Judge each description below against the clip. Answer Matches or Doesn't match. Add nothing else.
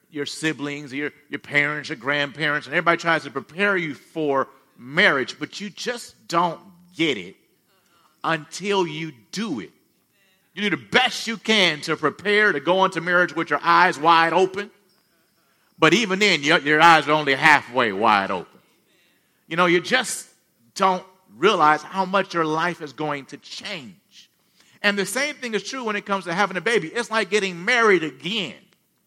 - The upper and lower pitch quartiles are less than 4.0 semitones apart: Doesn't match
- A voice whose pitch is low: Doesn't match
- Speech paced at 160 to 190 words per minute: Matches